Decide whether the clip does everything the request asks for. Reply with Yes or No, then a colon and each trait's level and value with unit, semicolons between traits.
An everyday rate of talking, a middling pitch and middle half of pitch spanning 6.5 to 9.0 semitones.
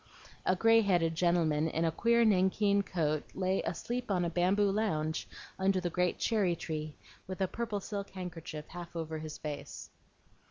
No: average, 165 wpm; medium, 180 Hz; average, 3.7 semitones